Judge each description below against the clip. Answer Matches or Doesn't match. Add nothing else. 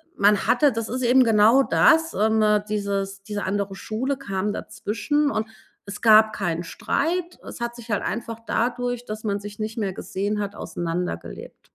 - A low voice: Doesn't match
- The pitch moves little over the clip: Doesn't match